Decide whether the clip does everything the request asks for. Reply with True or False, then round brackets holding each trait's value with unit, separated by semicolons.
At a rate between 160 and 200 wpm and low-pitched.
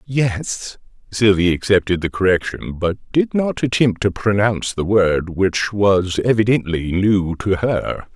False (140 wpm; 100 Hz)